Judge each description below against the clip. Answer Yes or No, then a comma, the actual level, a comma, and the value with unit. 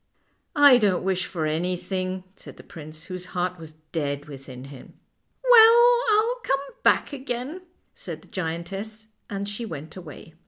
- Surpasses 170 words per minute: No, average, 160 wpm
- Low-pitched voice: No, medium, 185 Hz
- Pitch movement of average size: No, wide, 7.7 semitones